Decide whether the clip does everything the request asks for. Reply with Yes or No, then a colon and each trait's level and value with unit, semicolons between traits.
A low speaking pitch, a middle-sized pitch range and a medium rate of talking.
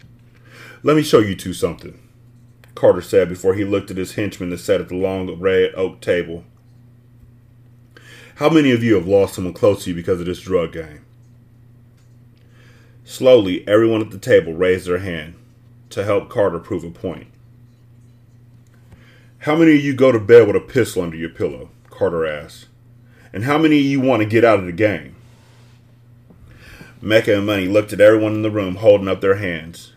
Yes: low, 120 Hz; average, 3.0 semitones; average, 180 wpm